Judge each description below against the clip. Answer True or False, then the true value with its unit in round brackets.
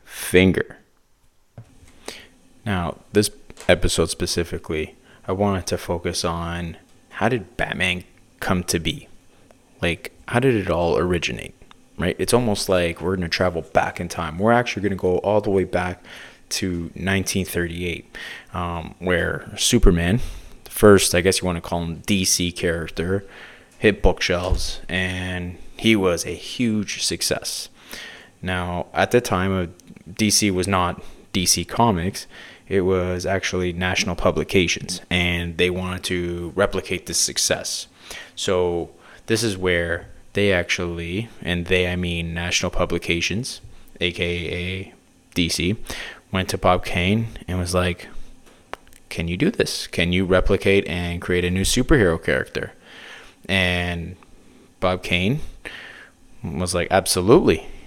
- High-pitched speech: False (90 Hz)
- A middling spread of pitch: False (1.9 semitones)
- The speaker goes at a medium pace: False (130 wpm)